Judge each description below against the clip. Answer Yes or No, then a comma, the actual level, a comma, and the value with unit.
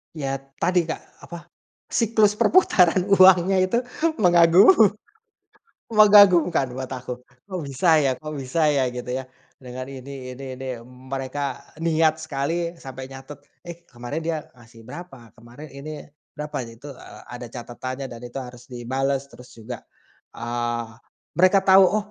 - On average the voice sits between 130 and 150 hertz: Yes, medium, 140 Hz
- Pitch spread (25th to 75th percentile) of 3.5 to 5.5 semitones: Yes, average, 5.2 semitones